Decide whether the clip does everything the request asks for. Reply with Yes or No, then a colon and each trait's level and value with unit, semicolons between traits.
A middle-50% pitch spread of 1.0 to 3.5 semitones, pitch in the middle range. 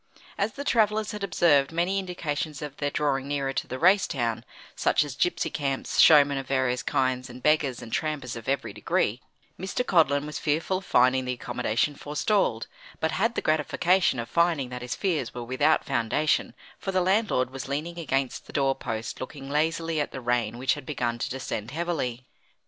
No: average, 4.6 semitones; medium, 145 Hz